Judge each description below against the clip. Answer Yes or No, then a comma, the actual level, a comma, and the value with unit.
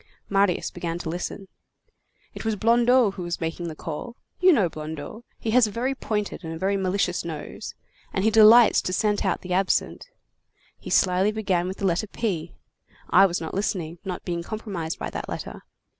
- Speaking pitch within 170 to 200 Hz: Yes, high, 190 Hz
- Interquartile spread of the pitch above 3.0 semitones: Yes, average, 4.0 semitones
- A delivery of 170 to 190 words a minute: Yes, average, 185 wpm